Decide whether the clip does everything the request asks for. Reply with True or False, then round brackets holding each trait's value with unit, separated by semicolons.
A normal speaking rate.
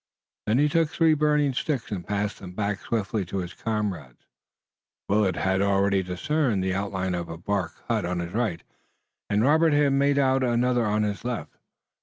True (180 wpm)